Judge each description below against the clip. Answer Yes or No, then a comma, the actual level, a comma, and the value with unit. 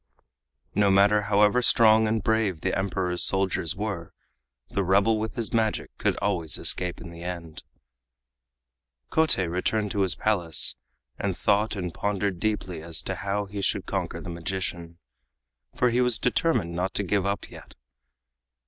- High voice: No, low, 100 Hz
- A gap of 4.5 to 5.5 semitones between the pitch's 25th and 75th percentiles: No, average, 3.2 semitones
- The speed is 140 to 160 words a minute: Yes, average, 155 wpm